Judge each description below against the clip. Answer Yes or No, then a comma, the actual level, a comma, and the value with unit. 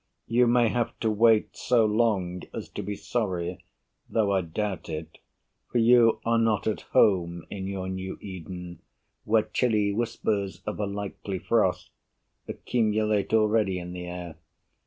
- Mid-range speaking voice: No, low, 105 Hz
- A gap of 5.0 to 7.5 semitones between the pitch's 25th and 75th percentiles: No, average, 3.3 semitones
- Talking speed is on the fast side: No, average, 150 wpm